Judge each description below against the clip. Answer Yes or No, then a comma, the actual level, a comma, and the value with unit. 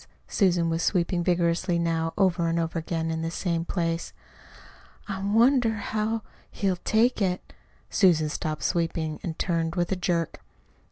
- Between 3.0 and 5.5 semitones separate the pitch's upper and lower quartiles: No, narrow, 2.6 semitones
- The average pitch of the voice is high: No, medium, 170 Hz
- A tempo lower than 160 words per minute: Yes, average, 150 wpm